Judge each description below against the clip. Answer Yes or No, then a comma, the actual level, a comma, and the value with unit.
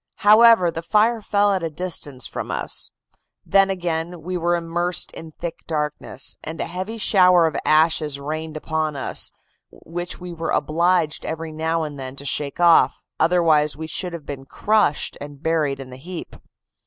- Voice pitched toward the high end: No, medium, 165 Hz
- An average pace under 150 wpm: No, average, 165 wpm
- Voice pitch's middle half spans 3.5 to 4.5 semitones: No, average, 2.8 semitones